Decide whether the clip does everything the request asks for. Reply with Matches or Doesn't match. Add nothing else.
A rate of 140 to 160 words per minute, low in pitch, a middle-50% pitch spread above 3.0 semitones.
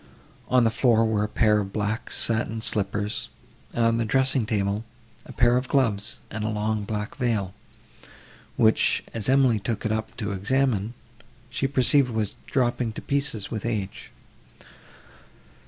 Doesn't match